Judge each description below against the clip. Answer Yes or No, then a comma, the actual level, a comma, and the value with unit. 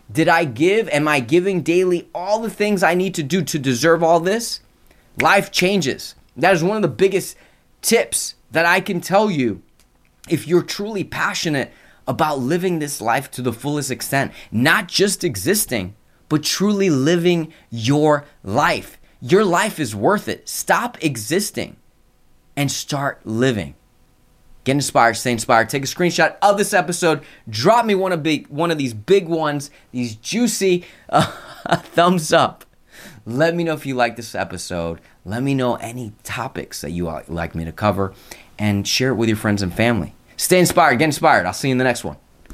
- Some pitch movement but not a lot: No, wide, 7.2 semitones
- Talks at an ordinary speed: Yes, average, 175 wpm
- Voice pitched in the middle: Yes, medium, 145 Hz